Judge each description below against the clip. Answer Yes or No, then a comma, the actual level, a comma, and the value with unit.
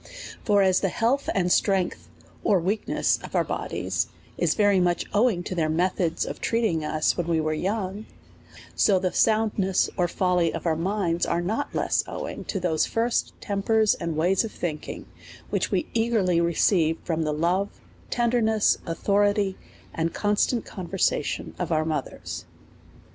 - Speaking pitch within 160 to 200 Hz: Yes, medium, 185 Hz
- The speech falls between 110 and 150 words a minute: No, average, 160 wpm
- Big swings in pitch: No, average, 3.7 semitones